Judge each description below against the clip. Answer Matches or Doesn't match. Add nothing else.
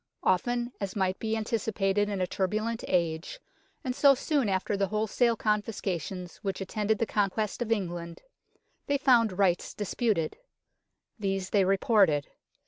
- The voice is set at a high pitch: Matches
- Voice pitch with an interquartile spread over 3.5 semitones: Doesn't match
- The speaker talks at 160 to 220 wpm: Doesn't match